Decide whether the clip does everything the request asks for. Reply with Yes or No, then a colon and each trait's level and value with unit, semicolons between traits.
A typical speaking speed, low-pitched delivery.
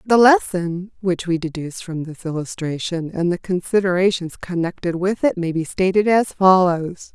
No: average, 160 wpm; medium, 180 Hz